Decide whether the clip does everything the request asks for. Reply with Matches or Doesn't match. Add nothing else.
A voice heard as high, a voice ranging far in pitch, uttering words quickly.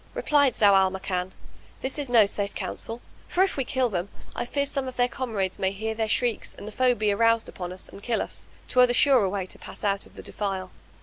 Doesn't match